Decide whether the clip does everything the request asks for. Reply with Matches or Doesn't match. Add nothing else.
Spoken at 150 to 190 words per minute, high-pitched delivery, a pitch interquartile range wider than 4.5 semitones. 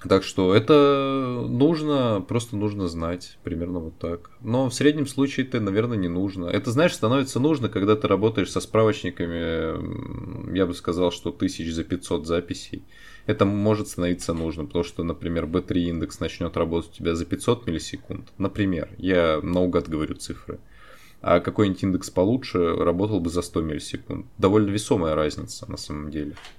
Doesn't match